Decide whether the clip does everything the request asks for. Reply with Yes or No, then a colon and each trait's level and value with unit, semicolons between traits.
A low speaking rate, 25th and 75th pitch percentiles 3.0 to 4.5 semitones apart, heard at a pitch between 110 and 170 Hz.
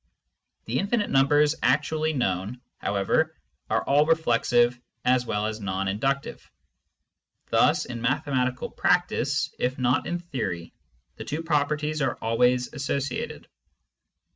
Yes: slow, 120 wpm; average, 4.1 semitones; low, 135 Hz